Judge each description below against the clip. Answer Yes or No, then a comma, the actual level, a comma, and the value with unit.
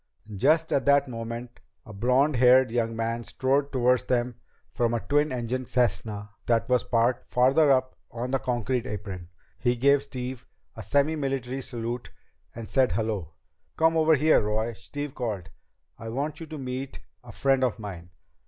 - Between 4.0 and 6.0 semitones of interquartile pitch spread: No, average, 3.0 semitones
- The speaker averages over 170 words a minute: No, average, 160 wpm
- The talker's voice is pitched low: Yes, low, 125 Hz